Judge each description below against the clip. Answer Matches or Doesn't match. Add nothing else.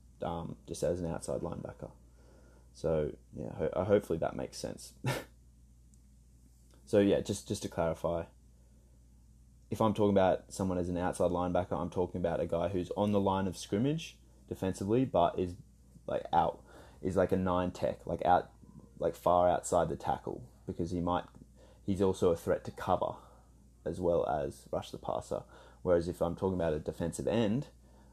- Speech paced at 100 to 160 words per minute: Doesn't match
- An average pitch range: Doesn't match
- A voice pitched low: Matches